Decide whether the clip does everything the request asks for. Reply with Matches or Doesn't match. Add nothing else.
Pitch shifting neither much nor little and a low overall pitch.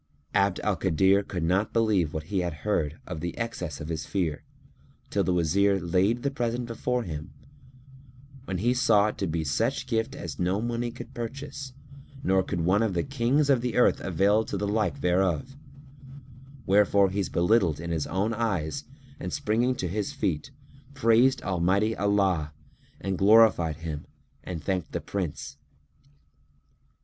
Matches